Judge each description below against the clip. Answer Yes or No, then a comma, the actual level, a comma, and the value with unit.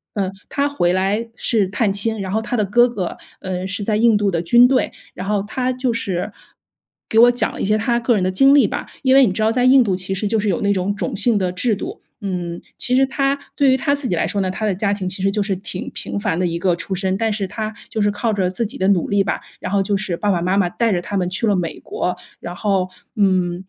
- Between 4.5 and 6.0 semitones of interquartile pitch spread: No, average, 3.6 semitones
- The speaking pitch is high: Yes, high, 200 Hz